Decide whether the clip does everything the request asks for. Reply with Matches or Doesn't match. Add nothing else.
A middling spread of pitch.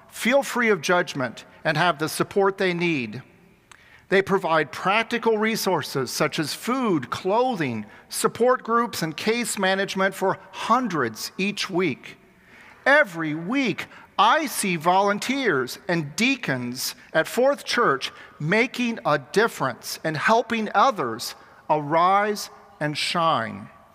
Doesn't match